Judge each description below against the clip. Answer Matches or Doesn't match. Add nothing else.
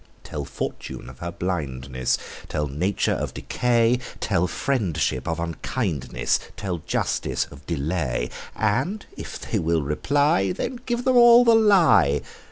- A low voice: Matches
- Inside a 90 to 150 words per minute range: Matches